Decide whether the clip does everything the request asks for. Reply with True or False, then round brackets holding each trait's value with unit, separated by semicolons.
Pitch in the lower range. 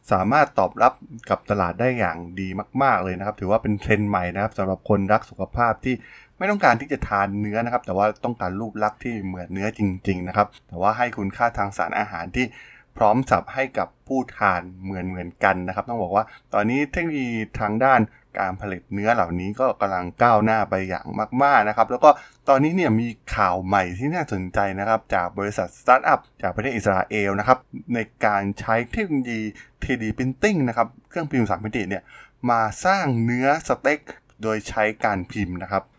True (110 Hz)